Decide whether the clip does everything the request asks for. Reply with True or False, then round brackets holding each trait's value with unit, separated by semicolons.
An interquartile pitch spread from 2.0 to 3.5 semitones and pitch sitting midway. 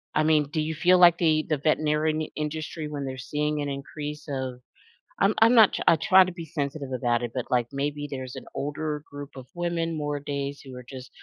True (2.4 semitones; 150 Hz)